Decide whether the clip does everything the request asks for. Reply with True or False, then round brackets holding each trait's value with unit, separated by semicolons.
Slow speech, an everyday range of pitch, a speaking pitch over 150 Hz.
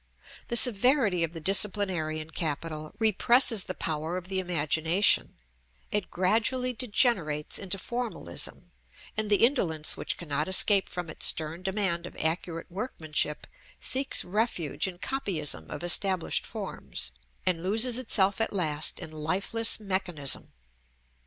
True (125 wpm; 5.0 semitones; 185 Hz)